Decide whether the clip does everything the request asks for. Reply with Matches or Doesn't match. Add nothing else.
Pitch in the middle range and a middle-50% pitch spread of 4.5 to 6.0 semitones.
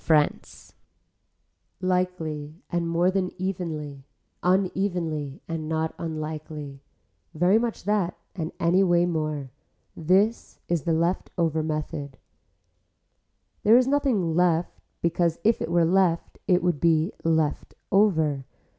Doesn't match